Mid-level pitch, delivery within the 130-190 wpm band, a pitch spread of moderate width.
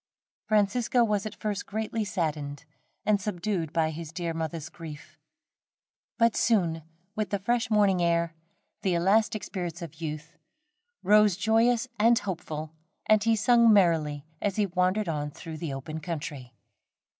Yes: medium, 180 Hz; average, 145 wpm; average, 4.9 semitones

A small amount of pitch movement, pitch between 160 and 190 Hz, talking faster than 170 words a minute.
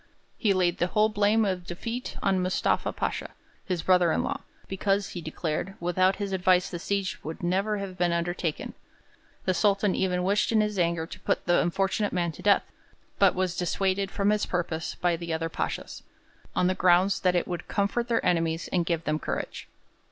Yes: narrow, 2.3 semitones; medium, 185 Hz; average, 190 wpm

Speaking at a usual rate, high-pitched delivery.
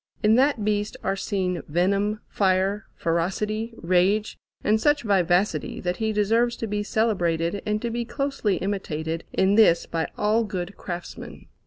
Yes: average, 150 wpm; high, 205 Hz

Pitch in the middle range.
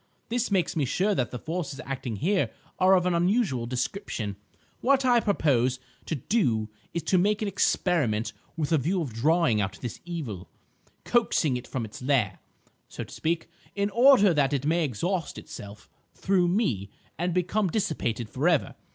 Yes: medium, 160 Hz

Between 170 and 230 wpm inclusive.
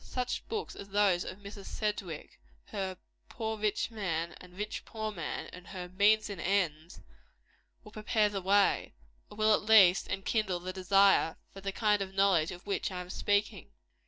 Yes: average, 175 wpm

